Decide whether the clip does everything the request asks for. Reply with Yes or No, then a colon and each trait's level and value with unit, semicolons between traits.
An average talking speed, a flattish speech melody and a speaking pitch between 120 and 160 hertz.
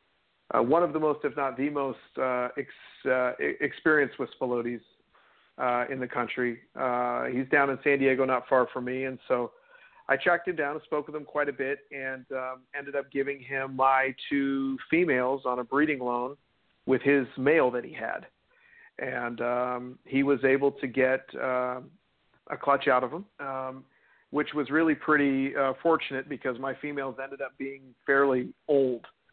Yes: average, 180 wpm; narrow, 1.9 semitones; low, 135 Hz